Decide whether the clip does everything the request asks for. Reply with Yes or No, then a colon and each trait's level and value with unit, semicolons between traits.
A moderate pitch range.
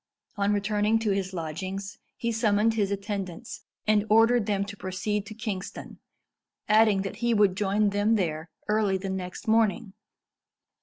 No: narrow, 2.0 semitones